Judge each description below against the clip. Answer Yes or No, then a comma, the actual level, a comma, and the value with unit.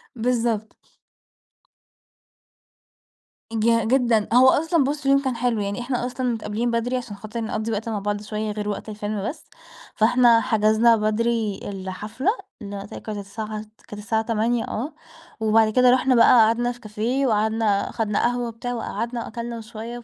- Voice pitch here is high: Yes, high, 225 Hz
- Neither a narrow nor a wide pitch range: No, narrow, 2.3 semitones